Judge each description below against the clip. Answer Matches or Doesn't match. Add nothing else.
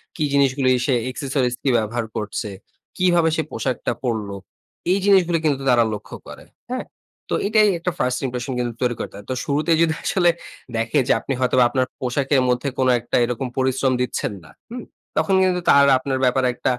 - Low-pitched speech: Matches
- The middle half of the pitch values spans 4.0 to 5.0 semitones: Matches